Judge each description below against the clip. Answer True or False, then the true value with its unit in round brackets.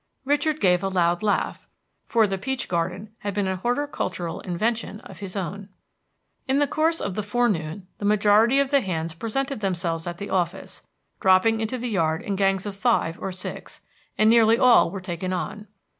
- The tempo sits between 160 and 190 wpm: True (185 wpm)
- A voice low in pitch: False (200 Hz)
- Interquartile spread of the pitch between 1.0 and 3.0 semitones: False (4.2 semitones)